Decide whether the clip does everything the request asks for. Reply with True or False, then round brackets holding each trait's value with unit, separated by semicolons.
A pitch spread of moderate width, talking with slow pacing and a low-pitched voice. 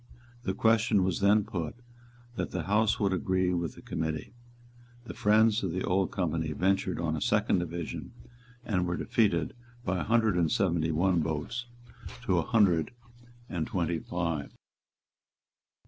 False (3.6 semitones; 150 wpm; 90 Hz)